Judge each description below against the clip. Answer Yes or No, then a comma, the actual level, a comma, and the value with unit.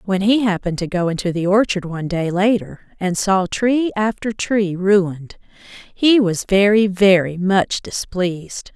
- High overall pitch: Yes, high, 195 Hz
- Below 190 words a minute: Yes, average, 160 wpm